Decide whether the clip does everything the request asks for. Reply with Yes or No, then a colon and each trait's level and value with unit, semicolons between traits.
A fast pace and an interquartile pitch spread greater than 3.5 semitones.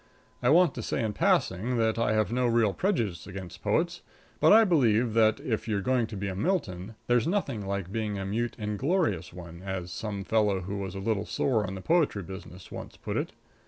Yes: fast, 210 wpm; average, 4.0 semitones